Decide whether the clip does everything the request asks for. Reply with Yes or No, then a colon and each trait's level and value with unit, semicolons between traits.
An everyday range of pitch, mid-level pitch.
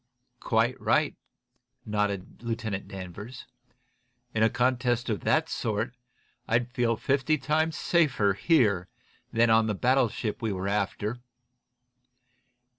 No: average, 3.6 semitones; low, 115 Hz